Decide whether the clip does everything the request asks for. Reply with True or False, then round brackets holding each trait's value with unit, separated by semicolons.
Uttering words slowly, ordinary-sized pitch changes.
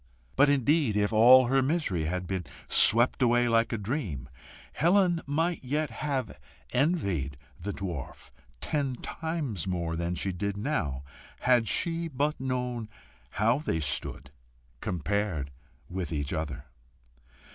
False (130 wpm; 8.1 semitones)